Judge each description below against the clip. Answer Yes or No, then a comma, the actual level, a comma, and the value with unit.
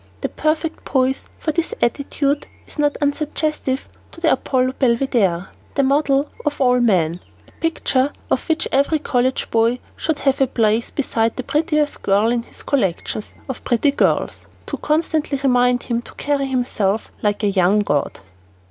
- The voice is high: Yes, very high, 260 Hz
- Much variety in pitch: No, average, 4.0 semitones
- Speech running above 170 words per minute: No, average, 160 wpm